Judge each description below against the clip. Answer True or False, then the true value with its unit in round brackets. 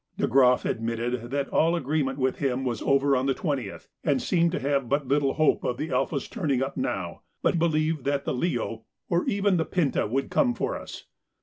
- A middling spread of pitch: True (3.8 semitones)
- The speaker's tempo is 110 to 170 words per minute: False (205 wpm)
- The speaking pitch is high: False (140 Hz)